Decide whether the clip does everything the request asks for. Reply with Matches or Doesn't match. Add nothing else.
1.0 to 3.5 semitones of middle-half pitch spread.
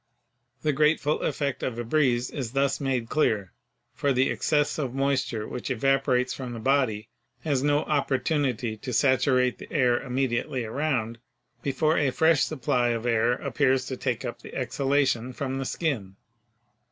Matches